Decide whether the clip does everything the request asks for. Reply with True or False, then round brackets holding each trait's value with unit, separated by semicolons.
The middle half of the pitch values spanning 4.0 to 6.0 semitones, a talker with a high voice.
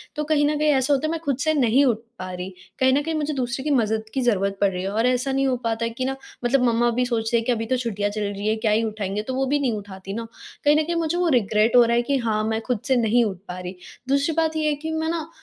True (4.6 semitones; 245 Hz)